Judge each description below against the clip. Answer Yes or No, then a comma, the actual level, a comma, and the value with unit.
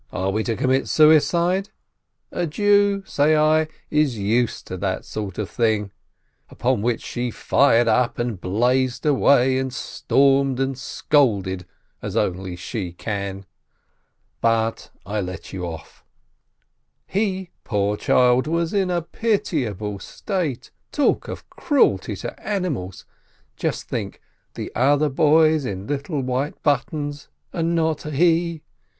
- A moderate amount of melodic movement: No, wide, 6.6 semitones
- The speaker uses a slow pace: Yes, slow, 130 wpm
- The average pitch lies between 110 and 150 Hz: Yes, low, 135 Hz